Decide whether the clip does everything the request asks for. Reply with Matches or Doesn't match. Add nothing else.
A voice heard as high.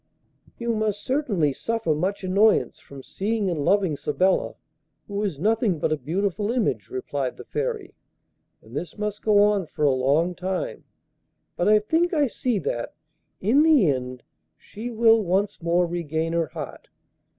Matches